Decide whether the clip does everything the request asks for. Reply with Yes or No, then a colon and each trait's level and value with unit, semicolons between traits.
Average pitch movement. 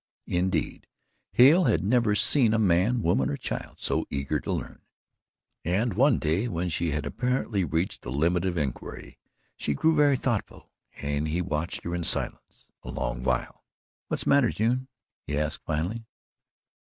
No: wide, 7.3 semitones